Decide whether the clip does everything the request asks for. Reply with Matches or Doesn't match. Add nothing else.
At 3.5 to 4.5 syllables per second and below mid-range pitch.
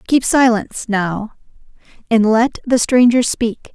Doesn't match